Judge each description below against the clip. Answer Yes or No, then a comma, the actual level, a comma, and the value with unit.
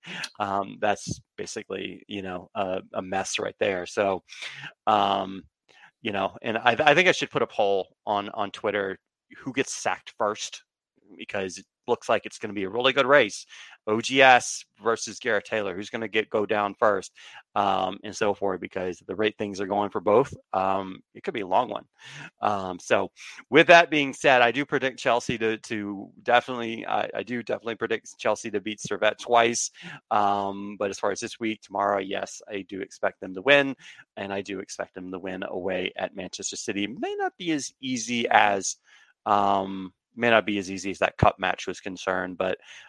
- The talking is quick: No, average, 195 wpm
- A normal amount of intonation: Yes, average, 3.4 semitones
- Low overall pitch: Yes, low, 105 Hz